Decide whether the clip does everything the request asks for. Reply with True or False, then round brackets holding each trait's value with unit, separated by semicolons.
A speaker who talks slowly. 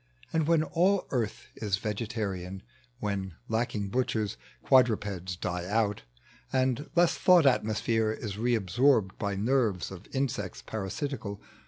True (130 wpm)